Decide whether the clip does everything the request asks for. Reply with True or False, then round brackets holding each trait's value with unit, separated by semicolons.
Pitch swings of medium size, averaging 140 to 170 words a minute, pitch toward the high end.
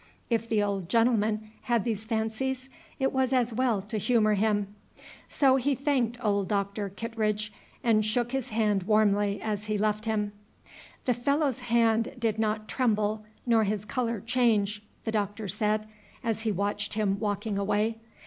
False (2.2 semitones; 160 wpm; 220 Hz)